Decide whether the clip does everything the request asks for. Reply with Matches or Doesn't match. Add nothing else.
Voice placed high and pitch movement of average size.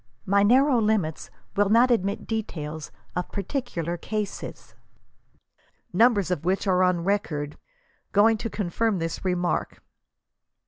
Matches